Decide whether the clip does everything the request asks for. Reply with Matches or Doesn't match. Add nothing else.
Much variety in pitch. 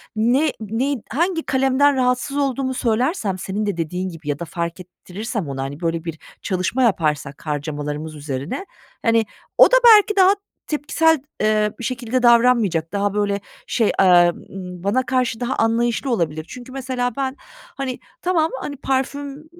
Matches